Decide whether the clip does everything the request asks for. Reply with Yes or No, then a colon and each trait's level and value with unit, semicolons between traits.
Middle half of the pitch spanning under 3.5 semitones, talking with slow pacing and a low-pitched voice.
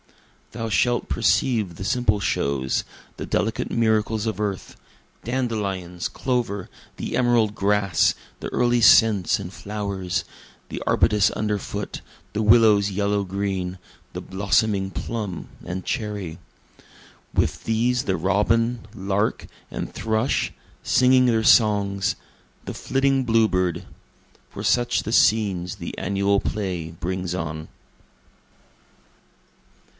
Yes: average, 3.0 semitones; slow, 110 wpm; low, 105 Hz